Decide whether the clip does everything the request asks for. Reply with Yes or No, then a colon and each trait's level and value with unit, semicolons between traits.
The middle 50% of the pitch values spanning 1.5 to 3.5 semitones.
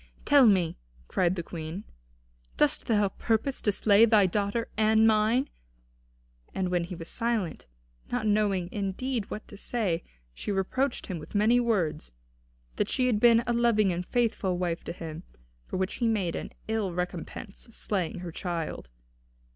No: average, 4.1 semitones